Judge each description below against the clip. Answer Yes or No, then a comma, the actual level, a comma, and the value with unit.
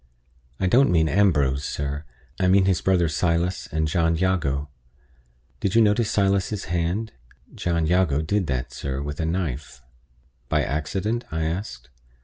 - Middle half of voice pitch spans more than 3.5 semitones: Yes, average, 4.5 semitones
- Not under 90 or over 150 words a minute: Yes, average, 145 wpm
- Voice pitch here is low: Yes, very low, 85 Hz